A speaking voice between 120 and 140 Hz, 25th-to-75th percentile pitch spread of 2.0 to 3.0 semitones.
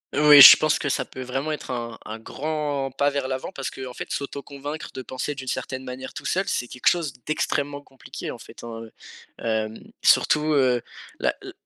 Yes: low, 135 Hz; narrow, 2.5 semitones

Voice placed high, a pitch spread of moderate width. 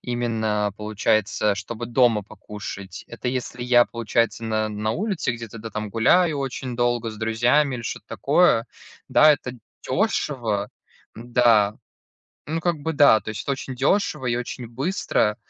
No: low, 120 Hz; average, 3.4 semitones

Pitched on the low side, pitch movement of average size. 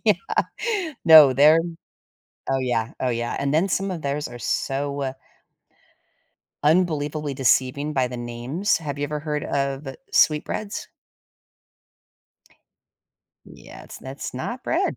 No: medium, 145 Hz; average, 3.0 semitones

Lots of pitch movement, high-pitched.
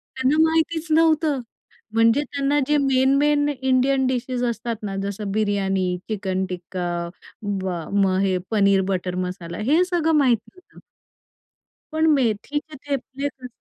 Yes: wide, 6.7 semitones; very high, 250 Hz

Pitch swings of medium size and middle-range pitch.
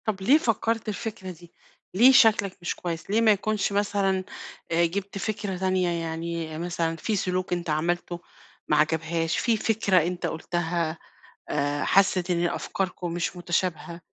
Yes: average, 3.1 semitones; medium, 180 Hz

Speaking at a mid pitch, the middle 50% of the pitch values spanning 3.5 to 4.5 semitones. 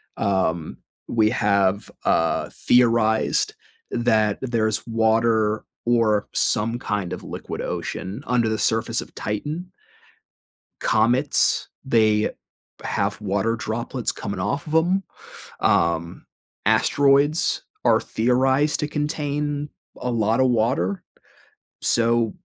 No: low, 115 Hz; average, 3.8 semitones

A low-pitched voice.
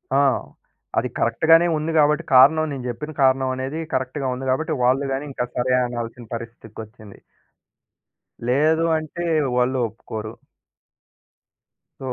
Yes: low, 130 Hz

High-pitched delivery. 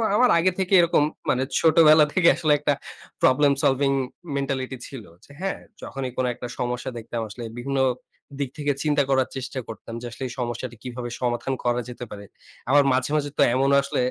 No: low, 135 Hz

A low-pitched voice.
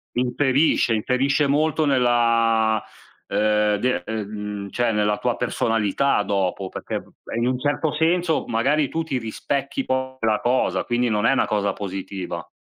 Yes: low, 120 Hz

